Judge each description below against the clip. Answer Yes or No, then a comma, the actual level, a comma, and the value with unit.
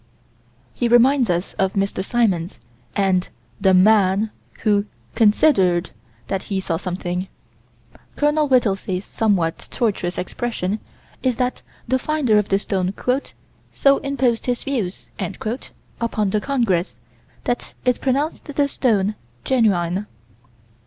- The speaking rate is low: Yes, slow, 115 wpm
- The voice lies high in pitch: Yes, high, 210 Hz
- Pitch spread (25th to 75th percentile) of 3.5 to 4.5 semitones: No, average, 4.9 semitones